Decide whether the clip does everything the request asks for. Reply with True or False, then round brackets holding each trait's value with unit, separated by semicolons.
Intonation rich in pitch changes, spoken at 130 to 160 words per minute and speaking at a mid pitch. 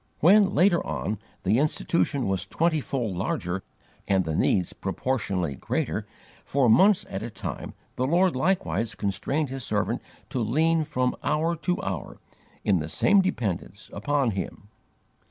False (8.3 semitones; 140 wpm; 125 Hz)